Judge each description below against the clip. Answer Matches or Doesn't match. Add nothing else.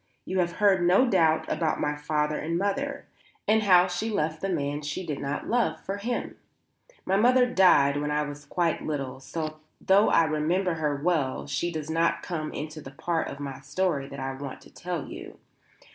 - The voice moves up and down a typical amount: Matches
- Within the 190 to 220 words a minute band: Matches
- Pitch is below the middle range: Doesn't match